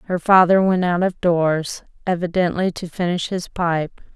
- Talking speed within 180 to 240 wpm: No, average, 160 wpm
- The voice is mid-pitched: Yes, medium, 175 Hz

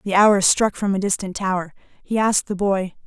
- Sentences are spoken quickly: Yes, fast, 215 wpm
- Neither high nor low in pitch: No, high, 195 Hz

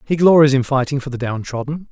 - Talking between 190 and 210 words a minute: No, fast, 220 wpm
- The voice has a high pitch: No, medium, 140 Hz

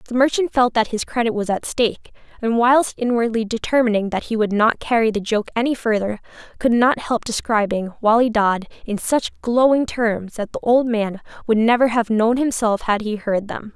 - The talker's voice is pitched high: Yes, high, 230 Hz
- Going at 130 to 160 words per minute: No, average, 195 wpm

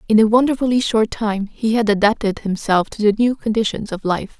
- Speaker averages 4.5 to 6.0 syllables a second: Yes, 5.5 syllables/s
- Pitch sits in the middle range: No, high, 215 Hz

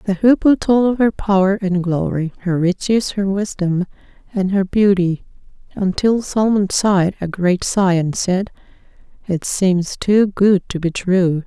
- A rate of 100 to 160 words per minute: Yes, average, 155 wpm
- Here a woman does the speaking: Yes, female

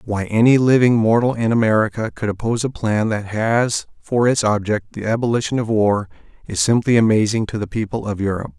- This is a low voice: Yes, low, 110 Hz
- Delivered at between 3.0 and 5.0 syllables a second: No, 5.7 syllables/s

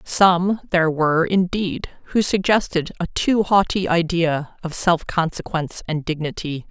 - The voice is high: No, medium, 175 Hz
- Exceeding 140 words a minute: No, slow, 135 wpm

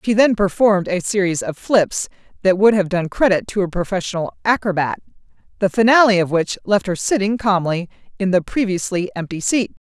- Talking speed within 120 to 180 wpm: Yes, average, 175 wpm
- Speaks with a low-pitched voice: No, high, 195 Hz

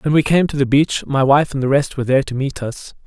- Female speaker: No, male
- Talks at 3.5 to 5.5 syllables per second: No, 6.1 syllables/s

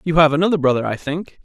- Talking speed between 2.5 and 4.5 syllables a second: No, 6.8 syllables/s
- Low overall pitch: No, medium, 155 Hz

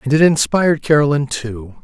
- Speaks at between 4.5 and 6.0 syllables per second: Yes, 5.3 syllables/s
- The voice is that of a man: Yes, male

